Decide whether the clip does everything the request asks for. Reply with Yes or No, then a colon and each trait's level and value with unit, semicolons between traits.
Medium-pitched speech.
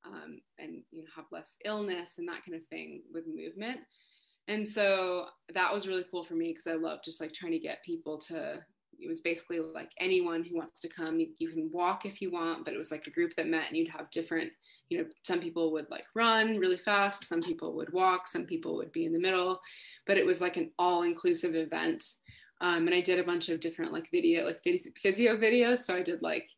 Yes: medium, 180 Hz